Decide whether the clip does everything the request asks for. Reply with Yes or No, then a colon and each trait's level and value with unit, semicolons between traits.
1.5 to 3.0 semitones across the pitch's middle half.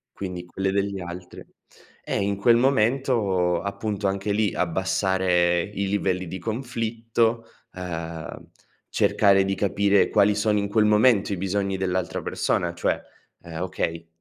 Yes: narrow, 2.5 semitones